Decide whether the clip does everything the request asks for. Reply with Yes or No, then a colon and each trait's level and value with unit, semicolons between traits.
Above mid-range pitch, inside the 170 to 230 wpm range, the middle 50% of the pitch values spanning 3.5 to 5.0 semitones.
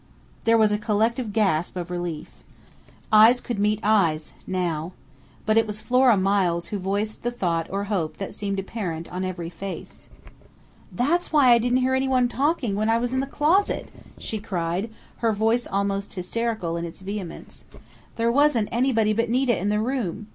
Yes: high, 210 Hz; average, 175 wpm; average, 4.3 semitones